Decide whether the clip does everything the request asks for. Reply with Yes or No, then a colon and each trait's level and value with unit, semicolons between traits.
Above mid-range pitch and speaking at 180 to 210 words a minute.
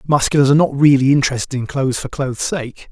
No: low, 135 Hz; fast, 205 wpm